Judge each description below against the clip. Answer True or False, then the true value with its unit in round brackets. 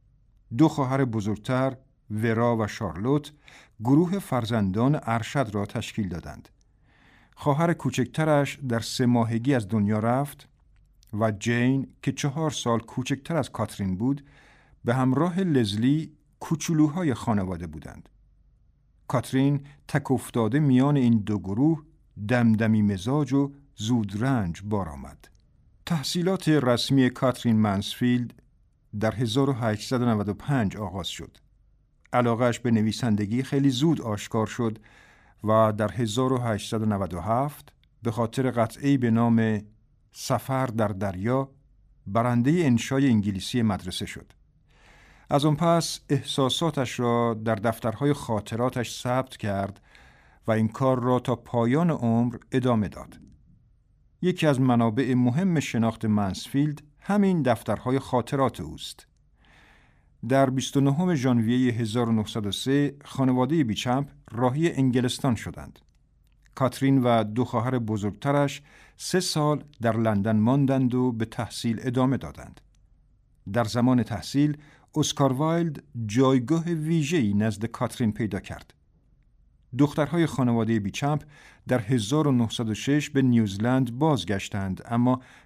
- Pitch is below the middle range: True (125 Hz)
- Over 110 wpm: False (105 wpm)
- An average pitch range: True (3.9 semitones)